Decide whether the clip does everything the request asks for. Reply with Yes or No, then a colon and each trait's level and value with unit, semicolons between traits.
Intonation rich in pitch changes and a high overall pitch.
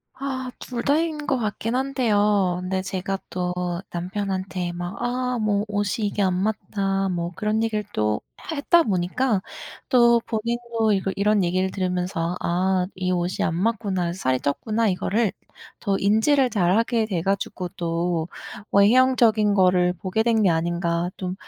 No: average, 3.9 semitones; high, 200 Hz